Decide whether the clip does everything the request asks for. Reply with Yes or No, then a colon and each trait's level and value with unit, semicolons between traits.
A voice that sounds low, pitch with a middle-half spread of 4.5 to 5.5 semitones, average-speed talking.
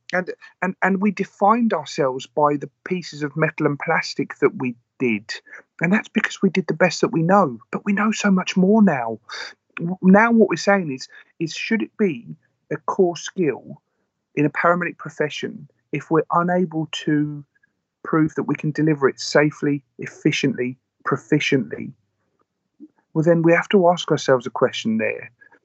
No: medium, 165 Hz; average, 5.2 semitones; average, 170 wpm